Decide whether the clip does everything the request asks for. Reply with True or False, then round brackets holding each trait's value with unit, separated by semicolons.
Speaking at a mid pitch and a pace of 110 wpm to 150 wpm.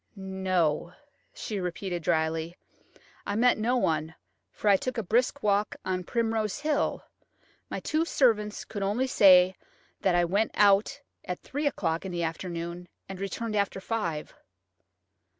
False (195 Hz; 140 wpm)